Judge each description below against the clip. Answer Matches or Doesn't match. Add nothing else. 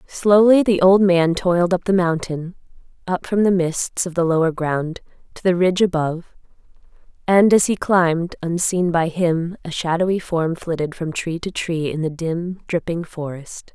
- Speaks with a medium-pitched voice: Matches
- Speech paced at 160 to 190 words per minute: Matches